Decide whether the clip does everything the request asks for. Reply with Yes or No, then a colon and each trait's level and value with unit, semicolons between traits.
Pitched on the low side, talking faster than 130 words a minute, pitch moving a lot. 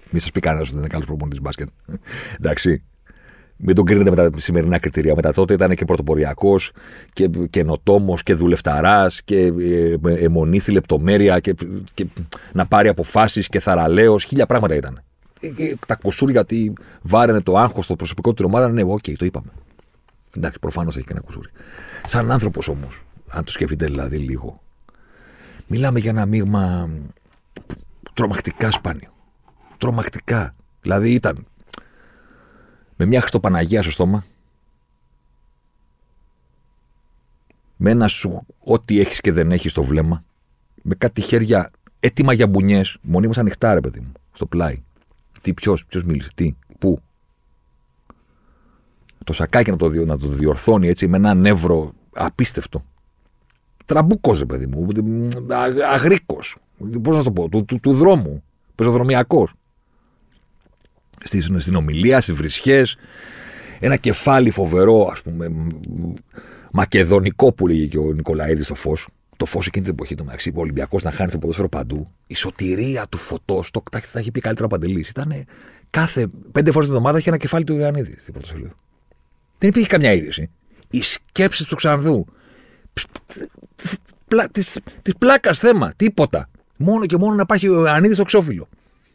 Yes: very low, 95 Hz; average, 150 wpm; wide, 6.9 semitones